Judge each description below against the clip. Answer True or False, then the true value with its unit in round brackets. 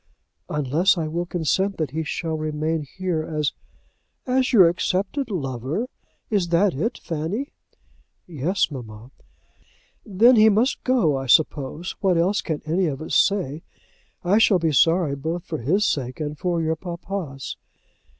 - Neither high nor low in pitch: True (165 Hz)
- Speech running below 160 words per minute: True (150 wpm)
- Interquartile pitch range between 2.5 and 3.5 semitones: False (4.3 semitones)